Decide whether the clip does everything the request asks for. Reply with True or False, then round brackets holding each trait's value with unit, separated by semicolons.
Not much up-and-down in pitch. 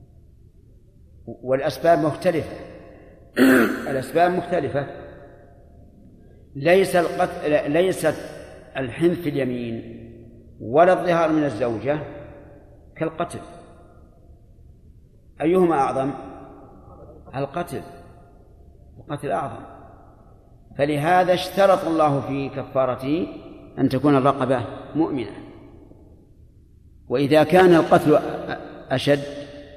False (5.4 semitones)